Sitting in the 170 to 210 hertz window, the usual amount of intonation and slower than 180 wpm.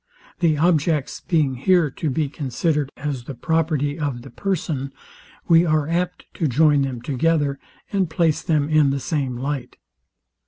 No: medium, 150 Hz; average, 3.0 semitones; average, 155 wpm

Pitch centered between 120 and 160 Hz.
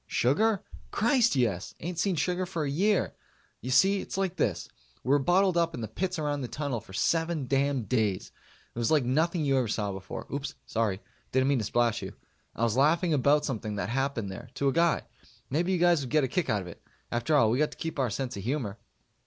Yes: medium, 140 Hz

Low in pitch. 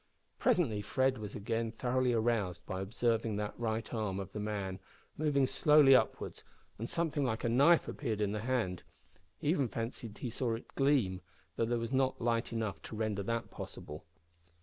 Yes: low, 115 Hz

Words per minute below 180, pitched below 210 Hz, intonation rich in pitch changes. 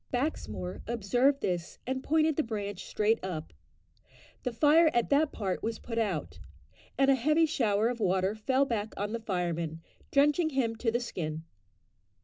No: average, 160 wpm; high, 225 Hz; wide, 6.4 semitones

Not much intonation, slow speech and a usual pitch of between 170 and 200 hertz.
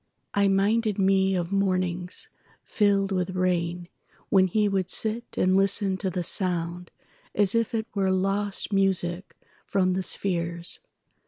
Yes: narrow, 1.8 semitones; slow, 130 wpm; high, 190 Hz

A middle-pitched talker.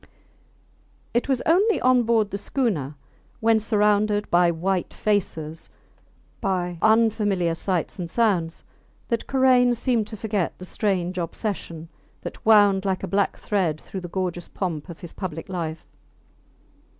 No: high, 195 Hz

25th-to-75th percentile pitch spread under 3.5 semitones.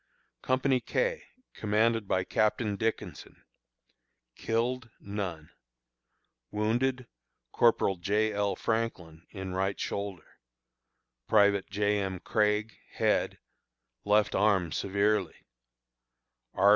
Yes: narrow, 2.6 semitones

